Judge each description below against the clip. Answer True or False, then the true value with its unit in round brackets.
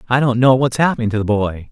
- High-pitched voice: False (120 Hz)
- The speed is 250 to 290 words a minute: True (280 wpm)